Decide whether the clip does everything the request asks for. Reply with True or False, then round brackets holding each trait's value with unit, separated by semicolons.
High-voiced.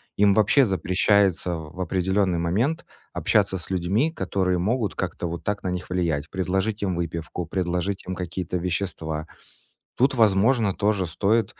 False (95 Hz)